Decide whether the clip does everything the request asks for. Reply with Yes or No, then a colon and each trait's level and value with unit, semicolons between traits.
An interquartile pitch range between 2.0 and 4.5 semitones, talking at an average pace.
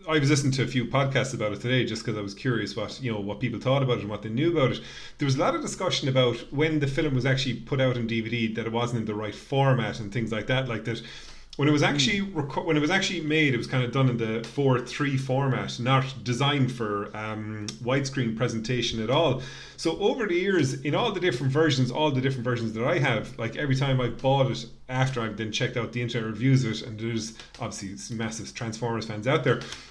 No: average, 3.1 semitones; fast, 255 wpm